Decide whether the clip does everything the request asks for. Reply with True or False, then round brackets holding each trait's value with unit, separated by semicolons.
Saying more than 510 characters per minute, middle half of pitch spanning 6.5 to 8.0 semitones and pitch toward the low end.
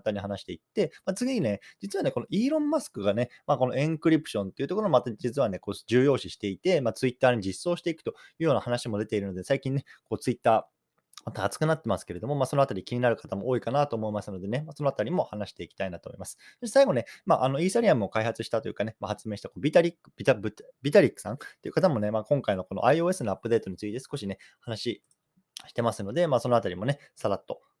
True (550 characters per minute; 7.0 semitones; 125 Hz)